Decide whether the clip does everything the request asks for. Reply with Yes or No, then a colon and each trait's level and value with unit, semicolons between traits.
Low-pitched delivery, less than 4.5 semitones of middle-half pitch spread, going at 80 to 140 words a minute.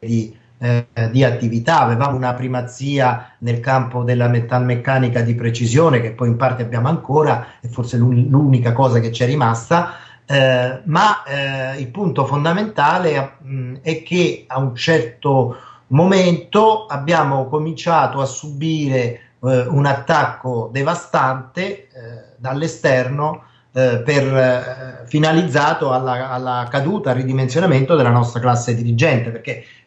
Yes: low, 130 Hz; average, 3.8 semitones; average, 130 wpm